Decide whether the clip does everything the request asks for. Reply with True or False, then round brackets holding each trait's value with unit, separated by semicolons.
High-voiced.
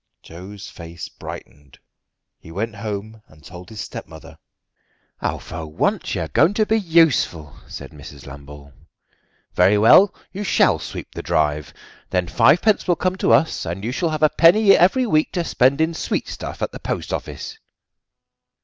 False (105 Hz)